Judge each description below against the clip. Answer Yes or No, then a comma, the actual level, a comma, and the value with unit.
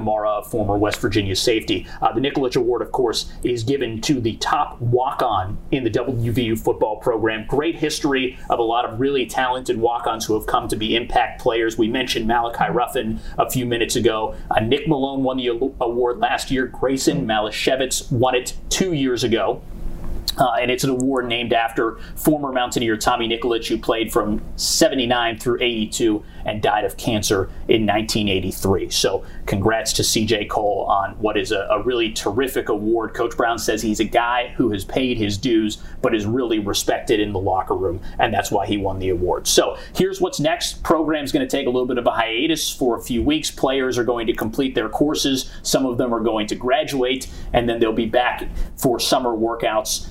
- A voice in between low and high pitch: No, low, 120 Hz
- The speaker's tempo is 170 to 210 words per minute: Yes, average, 200 wpm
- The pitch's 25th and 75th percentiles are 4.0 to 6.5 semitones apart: No, average, 3.3 semitones